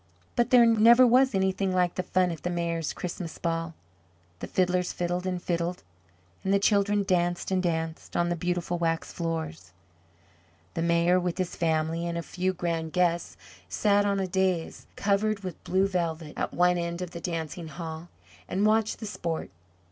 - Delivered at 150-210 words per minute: Yes, average, 175 wpm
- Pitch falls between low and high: Yes, medium, 175 Hz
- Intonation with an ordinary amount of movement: No, narrow, 2.2 semitones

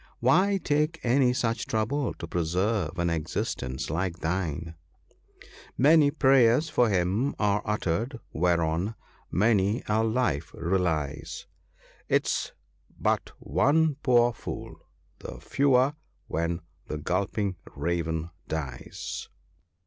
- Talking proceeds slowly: Yes, slow, 110 wpm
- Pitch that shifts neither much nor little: No, wide, 7.2 semitones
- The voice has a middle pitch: No, low, 100 Hz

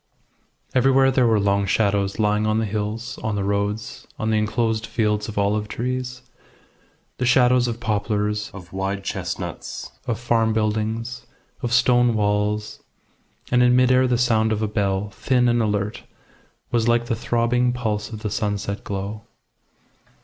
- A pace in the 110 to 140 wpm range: No, average, 155 wpm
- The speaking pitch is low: Yes, low, 110 Hz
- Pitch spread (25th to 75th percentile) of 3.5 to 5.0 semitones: No, average, 2.7 semitones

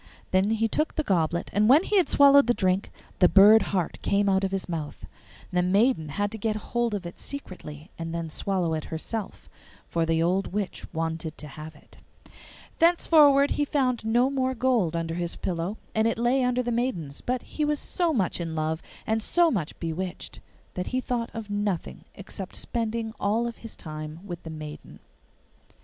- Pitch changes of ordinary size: No, wide, 6.3 semitones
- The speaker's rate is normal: Yes, average, 190 wpm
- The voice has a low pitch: No, high, 200 Hz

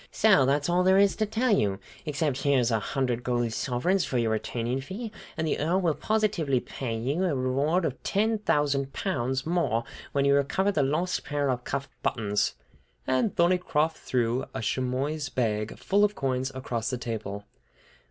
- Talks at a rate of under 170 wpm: No, average, 180 wpm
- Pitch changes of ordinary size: No, wide, 6.1 semitones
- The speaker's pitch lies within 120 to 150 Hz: Yes, medium, 140 Hz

